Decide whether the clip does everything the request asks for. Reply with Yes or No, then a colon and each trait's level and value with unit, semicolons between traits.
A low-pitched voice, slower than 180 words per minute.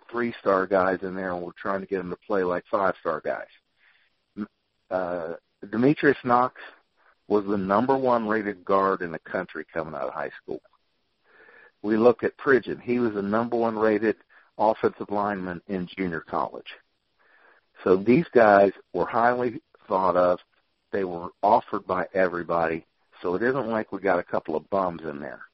Yes: low, 100 Hz; average, 170 wpm